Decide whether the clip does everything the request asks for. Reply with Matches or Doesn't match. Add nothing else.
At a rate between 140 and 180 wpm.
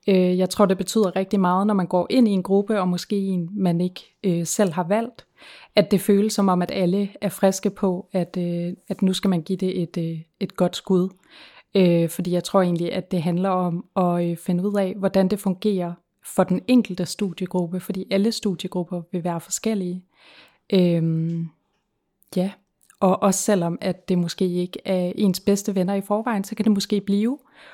Doesn't match